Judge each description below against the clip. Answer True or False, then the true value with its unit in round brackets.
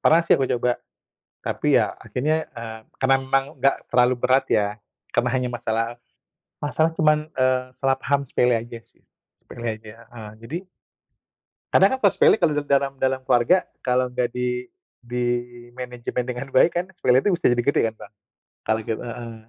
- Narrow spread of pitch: True (2.2 semitones)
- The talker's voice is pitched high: False (125 Hz)